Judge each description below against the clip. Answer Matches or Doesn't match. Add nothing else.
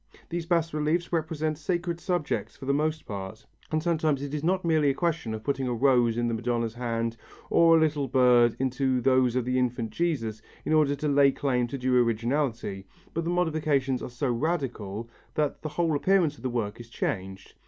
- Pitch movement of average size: Matches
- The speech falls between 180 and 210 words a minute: Matches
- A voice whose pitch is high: Doesn't match